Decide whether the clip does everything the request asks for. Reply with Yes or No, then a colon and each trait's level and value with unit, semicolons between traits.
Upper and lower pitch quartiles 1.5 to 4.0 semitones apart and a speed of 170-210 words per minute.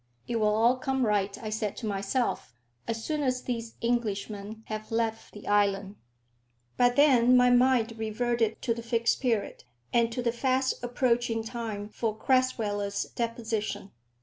No: narrow, 2.5 semitones; average, 150 wpm